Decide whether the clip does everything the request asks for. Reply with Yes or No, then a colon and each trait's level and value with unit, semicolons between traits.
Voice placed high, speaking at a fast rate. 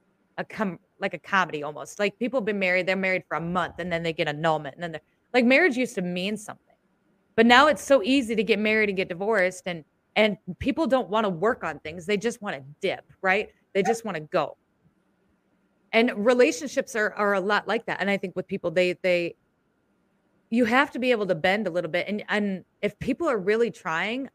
Yes: high, 200 Hz; fast, 230 wpm